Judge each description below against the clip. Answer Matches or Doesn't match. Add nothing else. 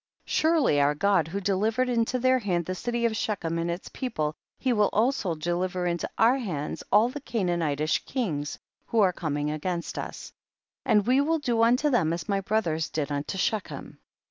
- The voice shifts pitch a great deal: Matches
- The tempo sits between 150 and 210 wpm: Matches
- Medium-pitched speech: Doesn't match